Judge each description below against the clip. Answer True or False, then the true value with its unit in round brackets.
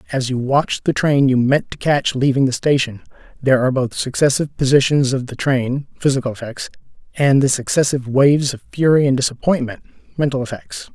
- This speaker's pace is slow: False (180 wpm)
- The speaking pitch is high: False (135 Hz)